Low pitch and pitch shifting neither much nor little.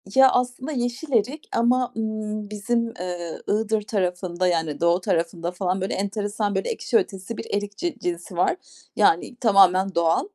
No: high, 205 Hz; average, 4.6 semitones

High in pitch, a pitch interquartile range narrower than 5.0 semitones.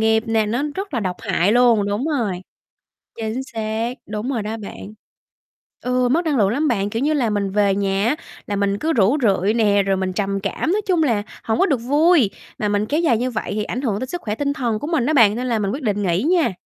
Yes: high, 225 Hz; average, 4.6 semitones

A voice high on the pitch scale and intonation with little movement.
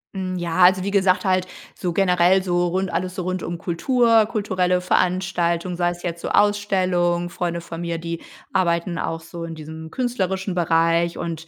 No: medium, 180 Hz; narrow, 1.8 semitones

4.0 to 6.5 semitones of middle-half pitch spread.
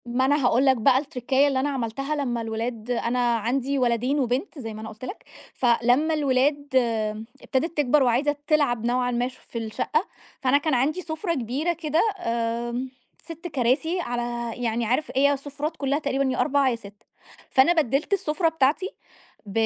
No: average, 3.6 semitones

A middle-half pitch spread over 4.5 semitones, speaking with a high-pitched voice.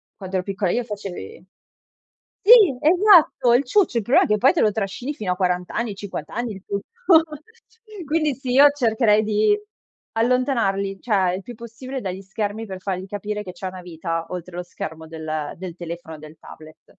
Yes: average, 5.2 semitones; high, 200 Hz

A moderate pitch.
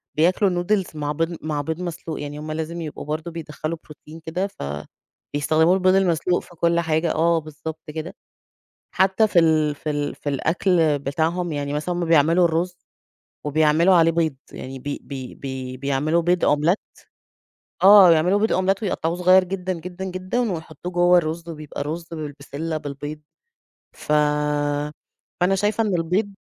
Yes: medium, 165 Hz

